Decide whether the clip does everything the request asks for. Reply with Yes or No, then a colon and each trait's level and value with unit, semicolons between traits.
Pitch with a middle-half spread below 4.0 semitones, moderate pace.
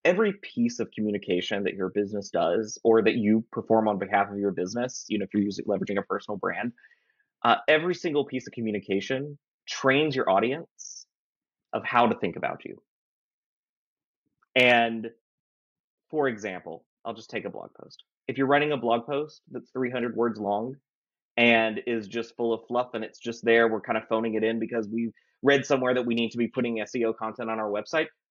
Yes: average, 3.2 semitones; average, 195 wpm